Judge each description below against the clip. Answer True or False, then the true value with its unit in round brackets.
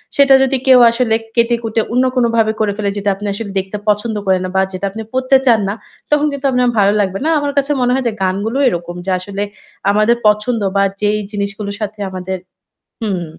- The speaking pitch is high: True (215 Hz)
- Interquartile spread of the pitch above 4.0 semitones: False (3.6 semitones)